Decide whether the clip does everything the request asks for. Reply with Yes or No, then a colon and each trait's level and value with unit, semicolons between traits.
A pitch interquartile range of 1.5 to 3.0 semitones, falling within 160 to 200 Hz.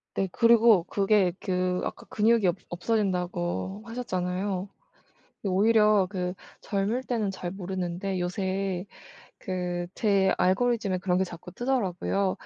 Yes: average, 2.7 semitones; high, 190 Hz